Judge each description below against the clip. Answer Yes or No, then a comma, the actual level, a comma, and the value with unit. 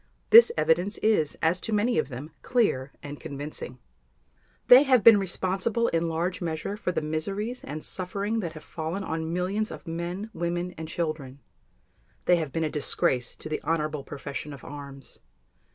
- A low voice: No, medium, 170 Hz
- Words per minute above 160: Yes, average, 170 wpm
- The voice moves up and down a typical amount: Yes, average, 4.7 semitones